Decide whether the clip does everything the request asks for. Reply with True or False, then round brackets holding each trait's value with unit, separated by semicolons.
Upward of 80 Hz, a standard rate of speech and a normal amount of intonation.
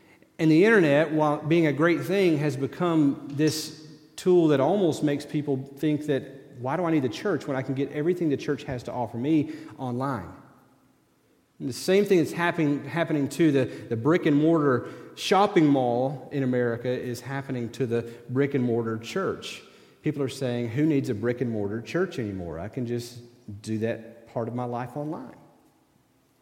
True (140 Hz; 185 wpm; 4.0 semitones)